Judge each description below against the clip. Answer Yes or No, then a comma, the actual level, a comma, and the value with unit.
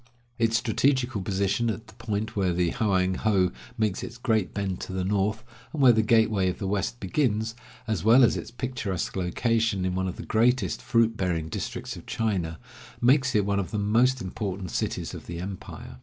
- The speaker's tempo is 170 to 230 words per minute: Yes, average, 195 wpm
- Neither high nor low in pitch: No, low, 105 Hz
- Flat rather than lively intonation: No, average, 3.6 semitones